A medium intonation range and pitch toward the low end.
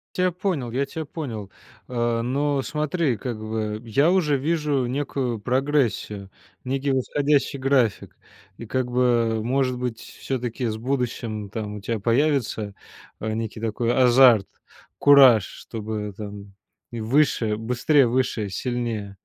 Yes: average, 3.9 semitones; low, 120 Hz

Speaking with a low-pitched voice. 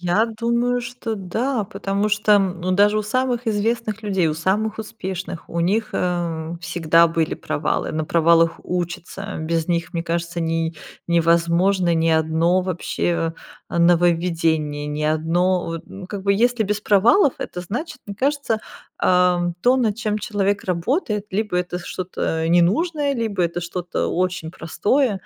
No: medium, 180 Hz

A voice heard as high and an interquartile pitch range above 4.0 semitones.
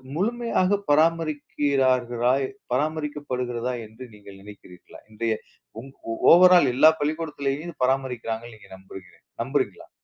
No: low, 130 Hz; average, 4.9 semitones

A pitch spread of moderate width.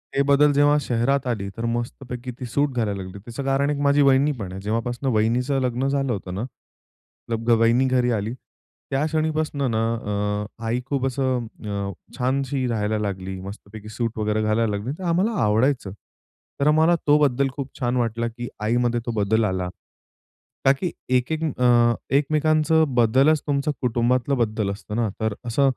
Yes: average, 4.1 semitones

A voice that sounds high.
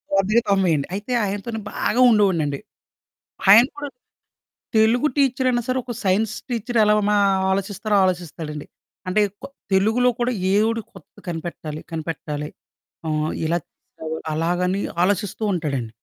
Yes: high, 195 Hz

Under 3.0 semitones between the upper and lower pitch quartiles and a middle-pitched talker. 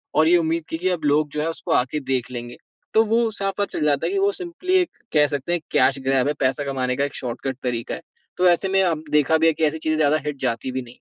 No: average, 4.5 semitones; medium, 150 Hz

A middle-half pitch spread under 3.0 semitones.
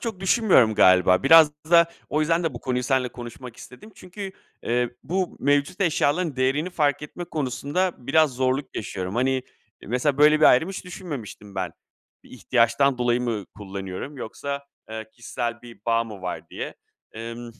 No: average, 5.0 semitones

